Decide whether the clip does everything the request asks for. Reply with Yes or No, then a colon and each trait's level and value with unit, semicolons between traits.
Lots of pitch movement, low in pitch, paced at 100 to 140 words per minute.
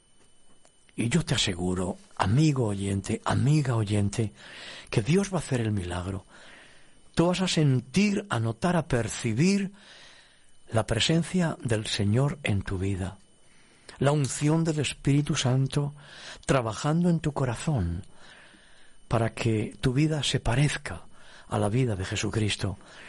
Yes: wide, 6.6 semitones; low, 125 Hz; average, 130 wpm